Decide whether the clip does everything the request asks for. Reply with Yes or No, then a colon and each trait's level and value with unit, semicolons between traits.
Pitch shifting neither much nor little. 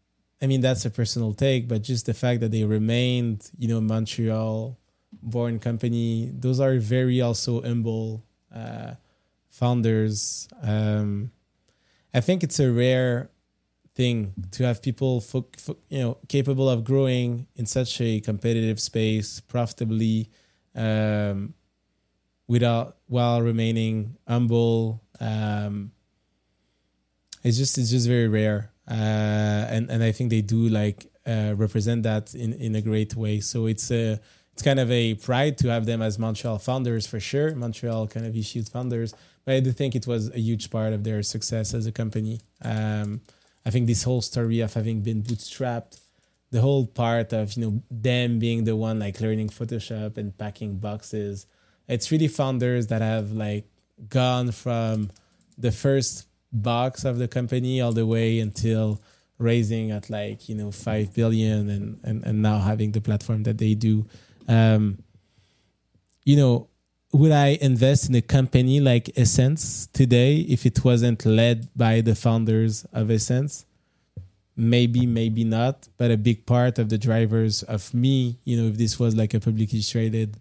No: narrow, 2.1 semitones